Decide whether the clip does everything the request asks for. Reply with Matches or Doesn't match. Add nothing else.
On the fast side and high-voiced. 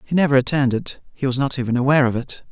Doesn't match